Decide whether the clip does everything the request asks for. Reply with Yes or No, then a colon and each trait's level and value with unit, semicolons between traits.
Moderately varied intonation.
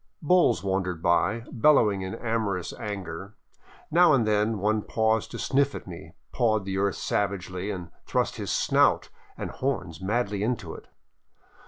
Yes: average, 3.4 semitones